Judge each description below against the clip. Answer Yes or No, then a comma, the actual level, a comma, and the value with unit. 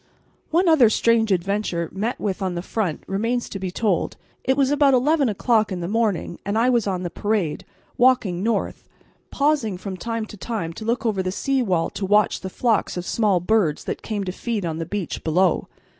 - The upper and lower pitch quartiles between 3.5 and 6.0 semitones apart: Yes, average, 4.1 semitones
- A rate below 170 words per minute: No, fast, 205 wpm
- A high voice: Yes, high, 210 Hz